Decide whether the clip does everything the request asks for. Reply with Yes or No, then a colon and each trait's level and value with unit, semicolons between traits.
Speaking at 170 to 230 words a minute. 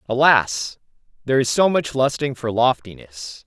No: average, 140 wpm